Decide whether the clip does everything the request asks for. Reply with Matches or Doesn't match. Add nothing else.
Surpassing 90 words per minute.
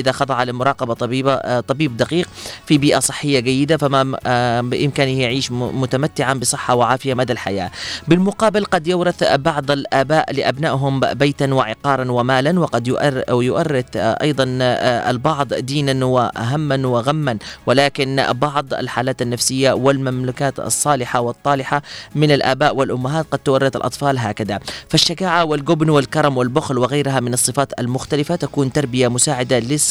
Matches